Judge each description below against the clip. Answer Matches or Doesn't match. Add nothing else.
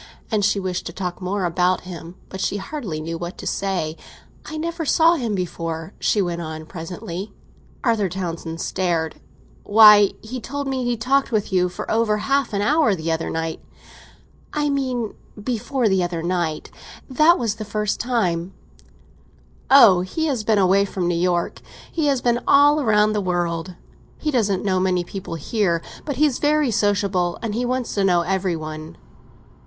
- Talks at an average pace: Matches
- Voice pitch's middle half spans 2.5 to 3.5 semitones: Doesn't match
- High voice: Matches